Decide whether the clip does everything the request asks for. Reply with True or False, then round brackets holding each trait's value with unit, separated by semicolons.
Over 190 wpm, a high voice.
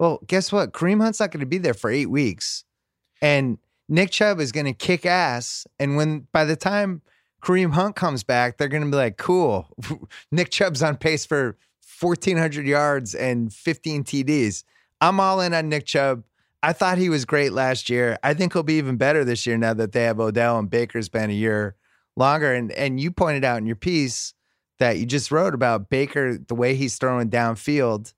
False (205 wpm; 140 Hz)